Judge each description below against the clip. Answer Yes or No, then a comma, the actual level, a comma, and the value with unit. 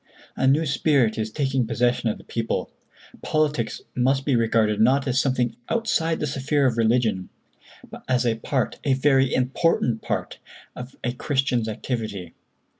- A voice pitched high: No, low, 125 Hz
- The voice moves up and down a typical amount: Yes, average, 3.1 semitones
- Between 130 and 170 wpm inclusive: Yes, average, 145 wpm